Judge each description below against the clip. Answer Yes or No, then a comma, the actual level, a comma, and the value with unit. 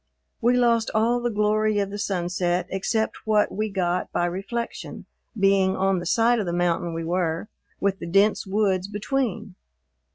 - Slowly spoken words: No, average, 165 wpm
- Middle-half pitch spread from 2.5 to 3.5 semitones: Yes, average, 3.2 semitones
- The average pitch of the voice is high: Yes, high, 200 Hz